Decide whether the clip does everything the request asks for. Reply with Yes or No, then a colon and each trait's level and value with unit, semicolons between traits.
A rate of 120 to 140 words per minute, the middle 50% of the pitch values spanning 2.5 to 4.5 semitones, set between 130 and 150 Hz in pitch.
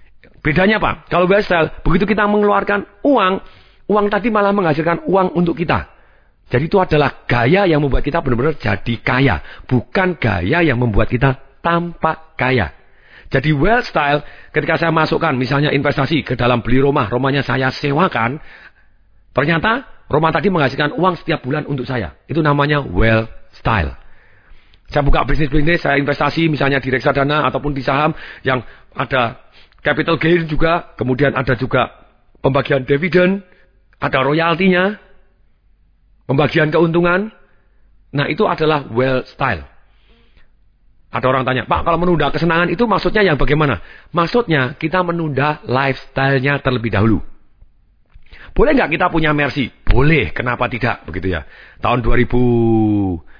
No: average, 135 wpm; wide, 5.4 semitones; medium, 140 Hz